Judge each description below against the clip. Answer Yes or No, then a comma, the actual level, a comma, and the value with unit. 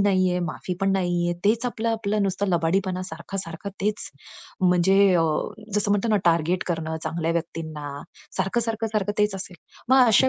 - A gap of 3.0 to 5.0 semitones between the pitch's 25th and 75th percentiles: Yes, average, 3.3 semitones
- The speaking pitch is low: No, high, 190 Hz